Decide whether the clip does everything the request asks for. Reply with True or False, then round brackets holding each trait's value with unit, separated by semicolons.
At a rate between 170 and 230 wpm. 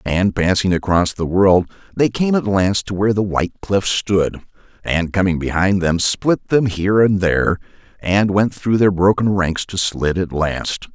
True (185 wpm)